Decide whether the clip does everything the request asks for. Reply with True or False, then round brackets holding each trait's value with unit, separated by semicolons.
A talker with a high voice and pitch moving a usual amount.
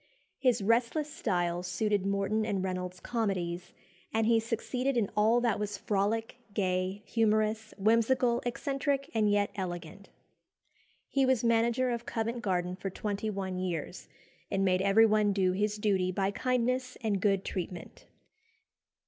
True (210 Hz; 3.5 semitones)